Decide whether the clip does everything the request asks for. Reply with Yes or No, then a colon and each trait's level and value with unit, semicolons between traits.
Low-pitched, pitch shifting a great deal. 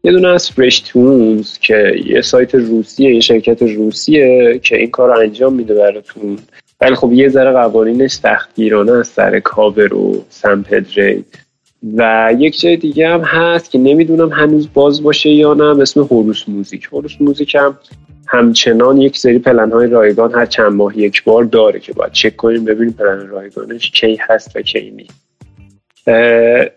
No: low, 120 Hz; average, 4.4 semitones